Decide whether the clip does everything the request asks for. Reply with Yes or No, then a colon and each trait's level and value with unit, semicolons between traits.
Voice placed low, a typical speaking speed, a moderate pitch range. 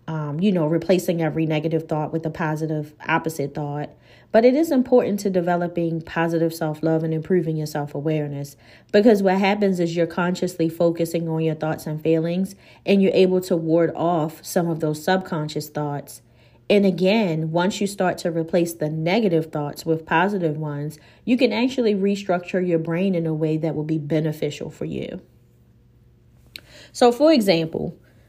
No: medium, 165 Hz; average, 170 wpm; average, 3.1 semitones